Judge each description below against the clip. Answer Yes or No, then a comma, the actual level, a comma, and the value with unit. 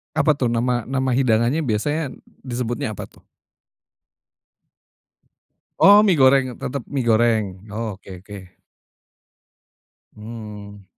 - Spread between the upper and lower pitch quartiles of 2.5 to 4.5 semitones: Yes, average, 3.7 semitones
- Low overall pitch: Yes, low, 120 Hz